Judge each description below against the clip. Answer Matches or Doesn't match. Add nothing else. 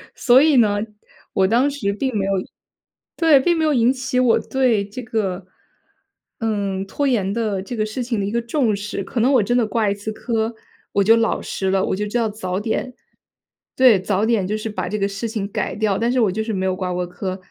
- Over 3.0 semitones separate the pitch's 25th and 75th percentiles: Matches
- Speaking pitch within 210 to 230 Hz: Matches